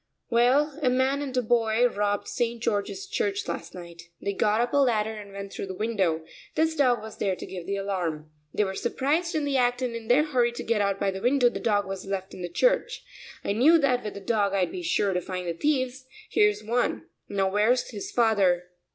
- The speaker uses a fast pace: Yes, fast, 230 wpm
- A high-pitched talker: Yes, high, 220 Hz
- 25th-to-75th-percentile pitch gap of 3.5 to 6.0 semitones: Yes, average, 4.6 semitones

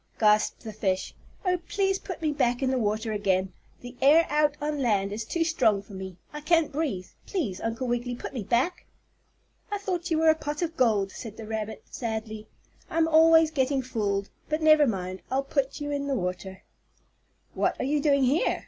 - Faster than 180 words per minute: Yes, average, 195 wpm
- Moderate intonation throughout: No, wide, 6.4 semitones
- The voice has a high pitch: Yes, very high, 260 Hz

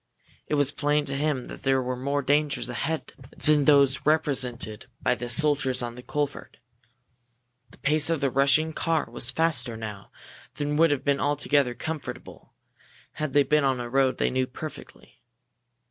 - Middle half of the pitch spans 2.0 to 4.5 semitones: Yes, average, 2.8 semitones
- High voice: No, medium, 140 Hz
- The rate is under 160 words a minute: No, average, 165 wpm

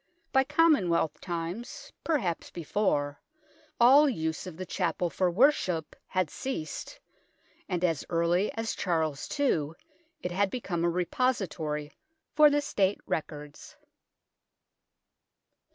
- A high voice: No, medium, 180 Hz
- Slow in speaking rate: Yes, slow, 115 wpm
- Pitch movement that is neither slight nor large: No, wide, 6.6 semitones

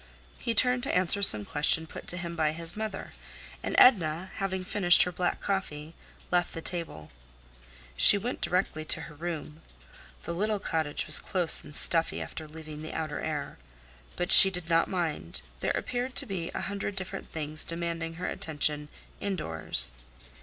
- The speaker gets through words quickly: No, average, 165 wpm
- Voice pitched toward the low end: No, medium, 170 Hz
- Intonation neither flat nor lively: Yes, average, 3.5 semitones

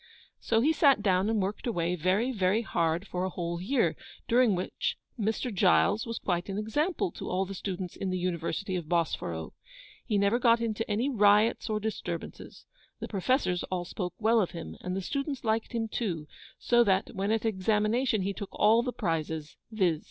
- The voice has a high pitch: Yes, high, 205 Hz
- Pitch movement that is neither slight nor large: Yes, average, 3.8 semitones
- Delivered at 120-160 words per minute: No, average, 190 wpm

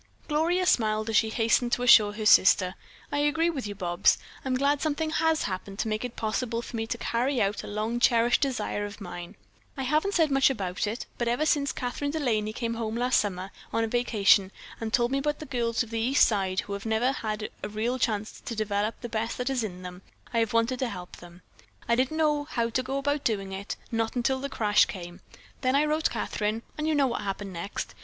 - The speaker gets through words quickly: Yes, fast, 230 wpm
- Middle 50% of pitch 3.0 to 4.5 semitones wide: Yes, average, 4.2 semitones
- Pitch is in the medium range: No, high, 230 Hz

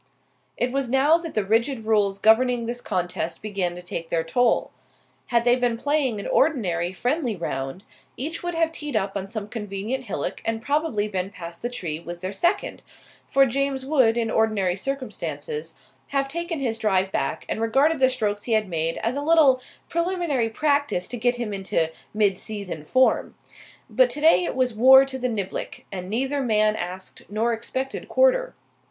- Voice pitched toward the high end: Yes, high, 230 Hz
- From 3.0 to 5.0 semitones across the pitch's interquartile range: No, wide, 5.5 semitones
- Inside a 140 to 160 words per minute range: No, average, 175 wpm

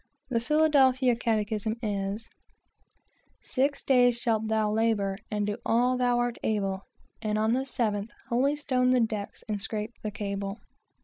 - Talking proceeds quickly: No, average, 140 wpm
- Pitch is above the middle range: Yes, high, 225 Hz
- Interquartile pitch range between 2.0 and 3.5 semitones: Yes, average, 3.1 semitones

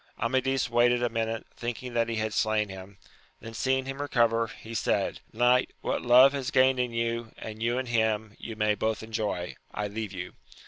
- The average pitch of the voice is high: No, low, 115 Hz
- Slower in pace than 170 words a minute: No, average, 190 wpm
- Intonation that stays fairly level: Yes, narrow, 2.2 semitones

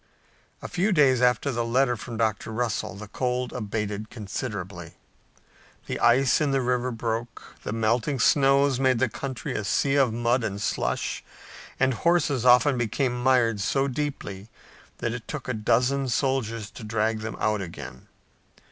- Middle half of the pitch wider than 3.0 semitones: Yes, average, 3.5 semitones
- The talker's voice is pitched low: Yes, low, 120 Hz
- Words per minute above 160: No, average, 155 wpm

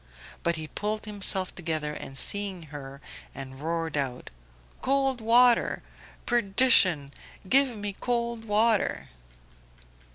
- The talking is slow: Yes, slow, 105 wpm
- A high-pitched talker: Yes, high, 200 Hz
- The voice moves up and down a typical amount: No, wide, 7.1 semitones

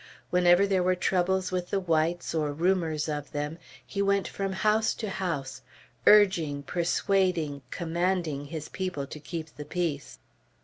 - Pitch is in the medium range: Yes, medium, 175 Hz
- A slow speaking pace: No, average, 145 wpm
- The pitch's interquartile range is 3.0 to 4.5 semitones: Yes, average, 3.8 semitones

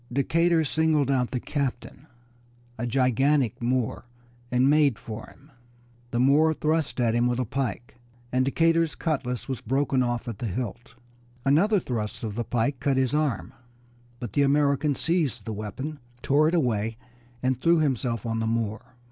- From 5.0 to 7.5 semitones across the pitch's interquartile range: No, average, 3.7 semitones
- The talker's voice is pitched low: Yes, low, 130 Hz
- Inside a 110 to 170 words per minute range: Yes, average, 165 wpm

